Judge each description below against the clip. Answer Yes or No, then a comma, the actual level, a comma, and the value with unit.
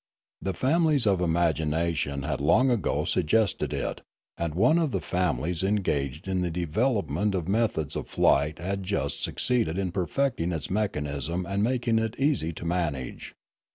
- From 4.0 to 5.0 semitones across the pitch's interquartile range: No, wide, 5.6 semitones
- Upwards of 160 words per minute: No, average, 155 wpm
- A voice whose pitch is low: Yes, very low, 90 Hz